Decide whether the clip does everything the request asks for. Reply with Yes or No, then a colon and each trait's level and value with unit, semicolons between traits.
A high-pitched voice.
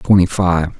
No: very low, 90 Hz